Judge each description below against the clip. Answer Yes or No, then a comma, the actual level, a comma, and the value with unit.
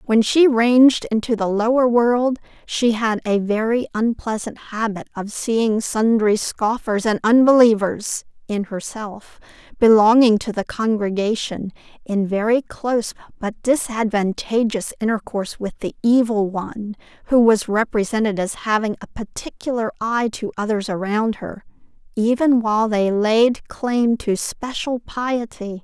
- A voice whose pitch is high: Yes, high, 225 Hz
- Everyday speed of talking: No, slow, 130 wpm